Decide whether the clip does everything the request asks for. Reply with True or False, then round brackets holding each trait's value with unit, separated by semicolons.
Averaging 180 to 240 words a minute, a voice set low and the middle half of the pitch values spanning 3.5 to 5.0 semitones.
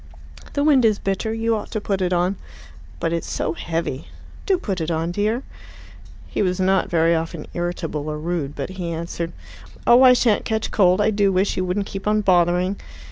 False (195 wpm; 185 Hz; 3.8 semitones)